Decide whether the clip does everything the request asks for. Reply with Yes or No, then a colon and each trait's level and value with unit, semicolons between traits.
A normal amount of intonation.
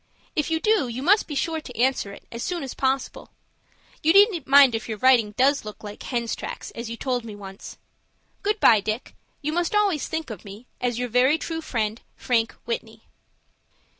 No: wide, 5.9 semitones